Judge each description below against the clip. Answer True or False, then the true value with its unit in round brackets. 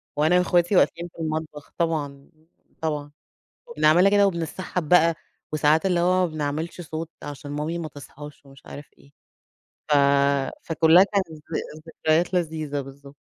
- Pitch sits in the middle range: True (160 Hz)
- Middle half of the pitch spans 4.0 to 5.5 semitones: False (2.9 semitones)